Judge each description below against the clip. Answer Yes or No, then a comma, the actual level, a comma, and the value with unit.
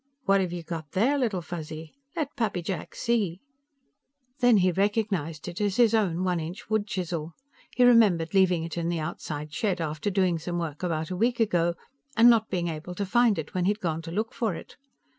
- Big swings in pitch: No, average, 4.3 semitones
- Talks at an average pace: No, fast, 210 wpm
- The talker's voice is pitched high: No, medium, 180 Hz